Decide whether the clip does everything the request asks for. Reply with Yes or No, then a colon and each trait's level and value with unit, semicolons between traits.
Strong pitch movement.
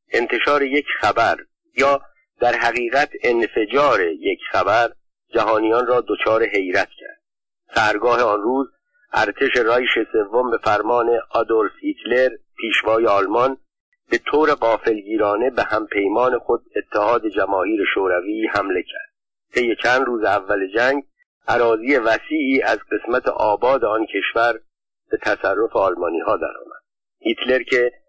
Yes: wide, 7.0 semitones